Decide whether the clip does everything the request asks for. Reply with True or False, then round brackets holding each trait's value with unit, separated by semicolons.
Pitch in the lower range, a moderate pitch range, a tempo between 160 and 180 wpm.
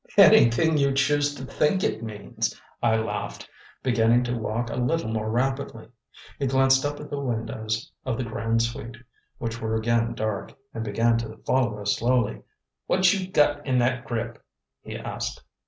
True (120 Hz; 3.2 semitones; 170 wpm)